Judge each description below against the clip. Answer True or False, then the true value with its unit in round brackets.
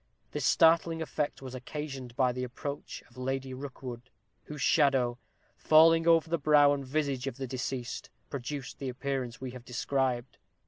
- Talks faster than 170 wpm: False (155 wpm)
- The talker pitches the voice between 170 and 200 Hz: False (135 Hz)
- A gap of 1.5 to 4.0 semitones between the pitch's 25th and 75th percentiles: True (2.7 semitones)